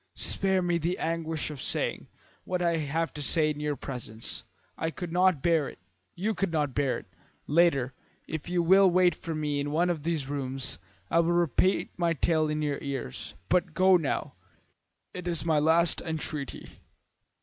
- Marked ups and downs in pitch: No, average, 3.1 semitones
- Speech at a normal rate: Yes, average, 180 wpm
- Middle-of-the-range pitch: Yes, medium, 160 Hz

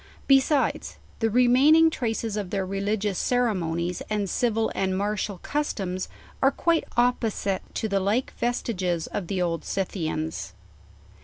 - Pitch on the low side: No, high, 205 Hz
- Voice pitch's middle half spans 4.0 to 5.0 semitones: Yes, average, 4.7 semitones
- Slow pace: Yes, slow, 130 wpm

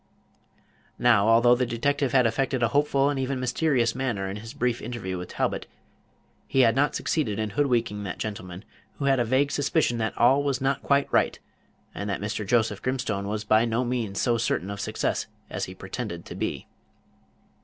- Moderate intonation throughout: Yes, average, 4.1 semitones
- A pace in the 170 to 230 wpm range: Yes, average, 185 wpm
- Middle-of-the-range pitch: No, low, 120 Hz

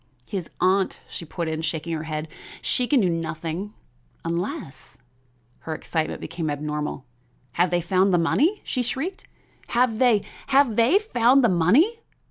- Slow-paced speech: No, average, 155 wpm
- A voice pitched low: No, medium, 180 Hz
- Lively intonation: Yes, wide, 7.4 semitones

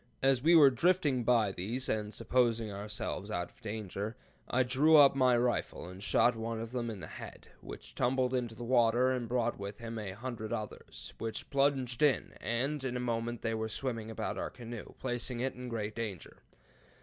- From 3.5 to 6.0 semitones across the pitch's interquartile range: No, narrow, 2.6 semitones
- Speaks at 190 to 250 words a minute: Yes, average, 195 wpm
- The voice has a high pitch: No, low, 120 Hz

